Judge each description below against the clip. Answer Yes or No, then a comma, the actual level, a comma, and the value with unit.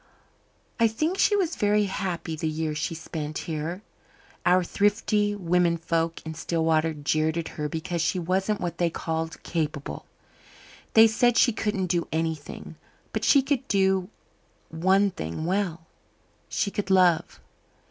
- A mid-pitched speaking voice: Yes, medium, 175 Hz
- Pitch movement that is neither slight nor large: Yes, average, 4.1 semitones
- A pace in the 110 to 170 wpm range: Yes, average, 145 wpm